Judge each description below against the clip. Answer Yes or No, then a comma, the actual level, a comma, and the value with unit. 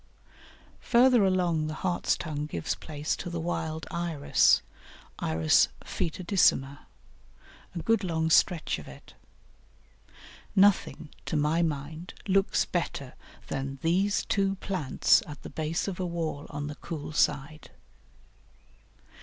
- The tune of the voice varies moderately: Yes, average, 3.7 semitones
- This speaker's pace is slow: Yes, slow, 120 wpm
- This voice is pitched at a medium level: Yes, medium, 160 Hz